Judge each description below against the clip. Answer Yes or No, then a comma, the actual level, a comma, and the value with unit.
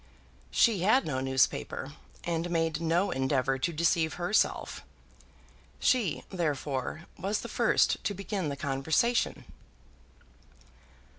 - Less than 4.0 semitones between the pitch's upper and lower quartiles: No, average, 5.2 semitones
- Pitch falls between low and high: Yes, medium, 165 Hz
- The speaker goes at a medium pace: No, slow, 105 wpm